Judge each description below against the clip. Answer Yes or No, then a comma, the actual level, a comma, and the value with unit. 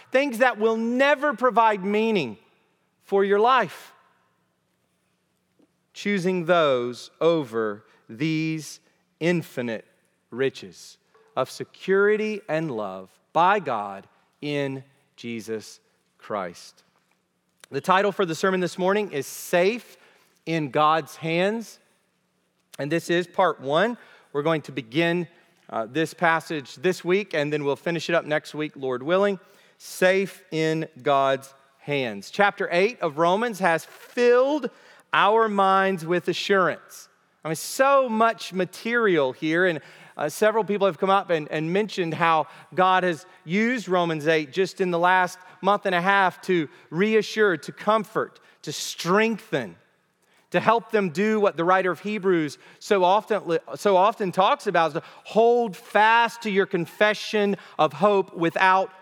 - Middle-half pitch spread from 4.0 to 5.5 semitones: Yes, average, 4.4 semitones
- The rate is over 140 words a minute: No, slow, 135 wpm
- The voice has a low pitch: No, medium, 185 Hz